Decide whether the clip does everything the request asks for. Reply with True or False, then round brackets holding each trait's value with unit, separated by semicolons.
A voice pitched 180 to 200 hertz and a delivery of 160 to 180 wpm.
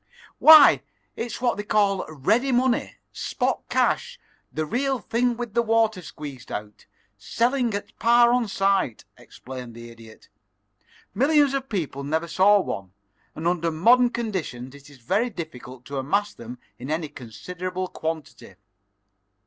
False (185 Hz; 140 wpm)